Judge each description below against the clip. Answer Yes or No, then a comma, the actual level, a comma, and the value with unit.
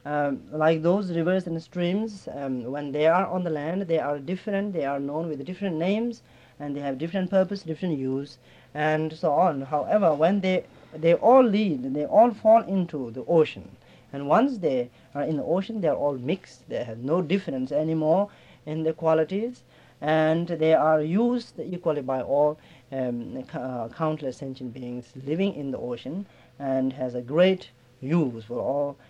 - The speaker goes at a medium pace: No, fast, 175 wpm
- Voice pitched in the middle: Yes, medium, 155 Hz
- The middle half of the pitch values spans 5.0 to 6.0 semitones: Yes, average, 5.3 semitones